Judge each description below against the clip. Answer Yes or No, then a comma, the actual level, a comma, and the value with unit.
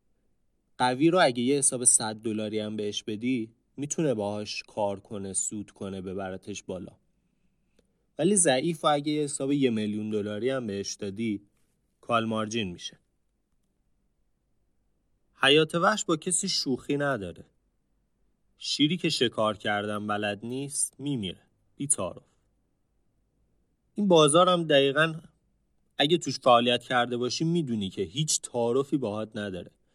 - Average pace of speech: Yes, average, 125 wpm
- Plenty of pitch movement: Yes, wide, 5.7 semitones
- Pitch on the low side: Yes, low, 120 Hz